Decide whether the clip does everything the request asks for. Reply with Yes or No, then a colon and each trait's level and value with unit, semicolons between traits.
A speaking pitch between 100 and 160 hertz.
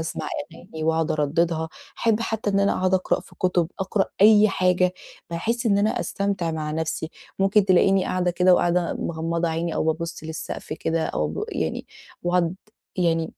No: medium, 175 Hz